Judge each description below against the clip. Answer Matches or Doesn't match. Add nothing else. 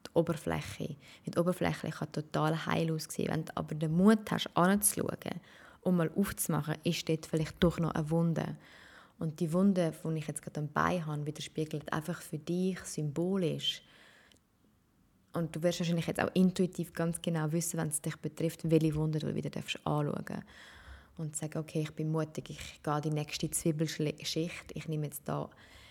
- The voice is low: Doesn't match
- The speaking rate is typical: Matches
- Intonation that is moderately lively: Doesn't match